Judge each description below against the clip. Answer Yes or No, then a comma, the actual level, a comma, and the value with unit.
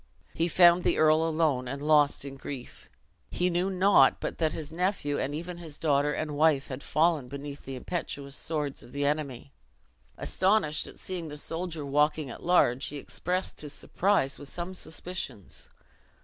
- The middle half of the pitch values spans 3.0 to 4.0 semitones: Yes, average, 3.5 semitones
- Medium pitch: Yes, medium, 150 Hz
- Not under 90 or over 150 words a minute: No, average, 170 wpm